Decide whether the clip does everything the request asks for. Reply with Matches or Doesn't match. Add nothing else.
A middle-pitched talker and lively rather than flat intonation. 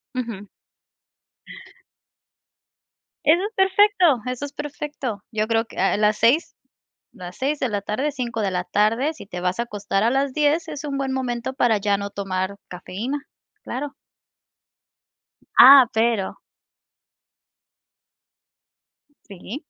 Doesn't match